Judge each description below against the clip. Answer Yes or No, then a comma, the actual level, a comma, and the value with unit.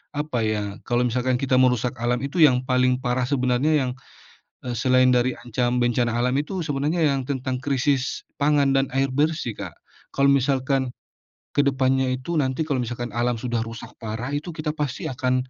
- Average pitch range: No, narrow, 2.2 semitones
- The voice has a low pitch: Yes, low, 130 Hz